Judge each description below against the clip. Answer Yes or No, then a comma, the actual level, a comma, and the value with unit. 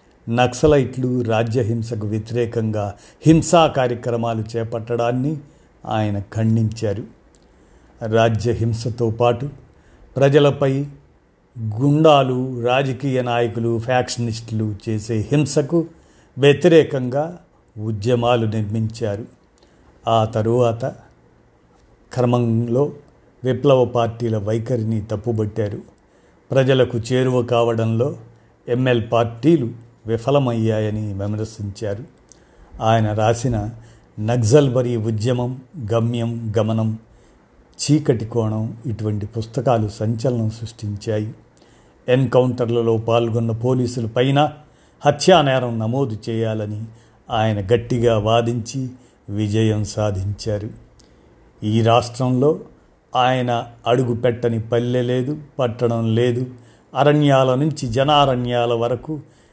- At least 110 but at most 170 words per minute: No, slow, 70 wpm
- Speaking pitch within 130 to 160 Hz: No, low, 120 Hz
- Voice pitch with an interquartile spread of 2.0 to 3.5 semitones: Yes, narrow, 2.4 semitones